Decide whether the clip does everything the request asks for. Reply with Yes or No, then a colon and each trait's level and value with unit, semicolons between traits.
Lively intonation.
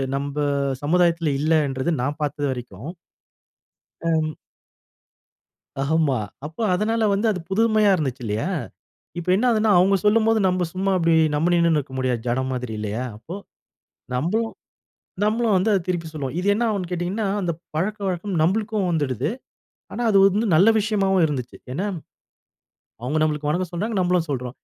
Yes: wide, 5.7 semitones